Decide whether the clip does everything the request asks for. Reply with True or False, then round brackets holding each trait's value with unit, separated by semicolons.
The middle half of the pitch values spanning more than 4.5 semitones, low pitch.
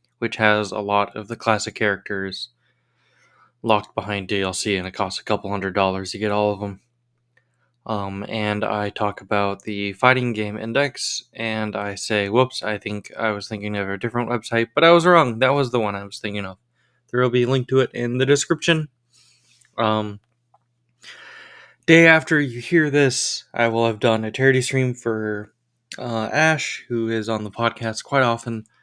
False (3.1 semitones; 115 Hz)